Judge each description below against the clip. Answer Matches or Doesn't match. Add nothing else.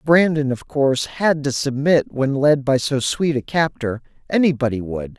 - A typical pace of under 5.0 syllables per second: Matches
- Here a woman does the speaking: Doesn't match